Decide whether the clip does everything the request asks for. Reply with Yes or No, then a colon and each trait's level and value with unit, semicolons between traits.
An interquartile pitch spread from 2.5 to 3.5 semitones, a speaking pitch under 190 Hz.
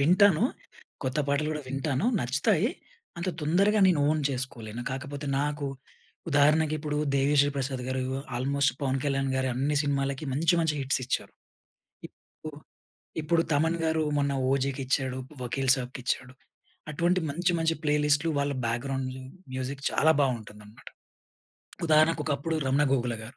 Yes: average, 2.9 semitones; medium, 140 Hz